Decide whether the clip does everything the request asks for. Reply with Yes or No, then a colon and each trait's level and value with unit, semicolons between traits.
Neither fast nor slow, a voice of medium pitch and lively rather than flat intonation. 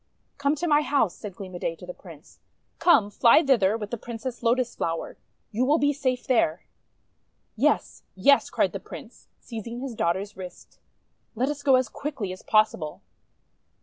No: average, 180 wpm; high, 230 Hz; wide, 6.1 semitones